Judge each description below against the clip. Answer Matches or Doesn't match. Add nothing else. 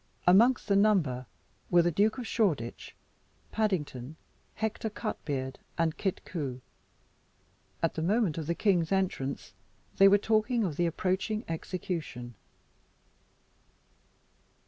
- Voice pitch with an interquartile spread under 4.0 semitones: Doesn't match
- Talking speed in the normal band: Doesn't match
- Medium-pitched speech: Matches